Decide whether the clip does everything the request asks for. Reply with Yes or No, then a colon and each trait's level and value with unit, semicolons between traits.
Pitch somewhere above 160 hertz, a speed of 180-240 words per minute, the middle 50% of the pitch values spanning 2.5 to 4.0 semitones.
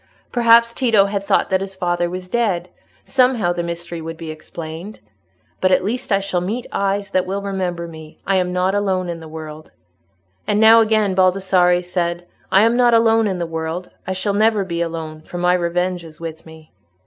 Yes: medium, 185 Hz; average, 195 wpm; average, 2.9 semitones